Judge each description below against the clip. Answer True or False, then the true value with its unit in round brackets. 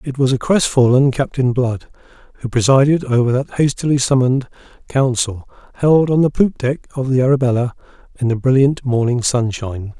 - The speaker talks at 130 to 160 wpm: True (155 wpm)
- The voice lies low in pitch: True (130 Hz)